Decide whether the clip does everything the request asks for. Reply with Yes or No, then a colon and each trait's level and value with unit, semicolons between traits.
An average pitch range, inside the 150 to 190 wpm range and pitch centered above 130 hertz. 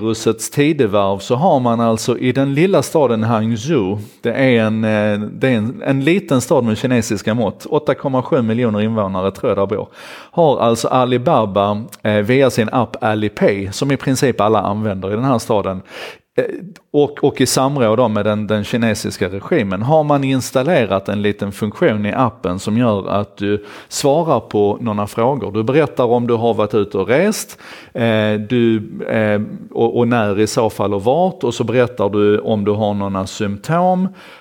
No: average, 3.7 semitones; average, 165 wpm; low, 110 Hz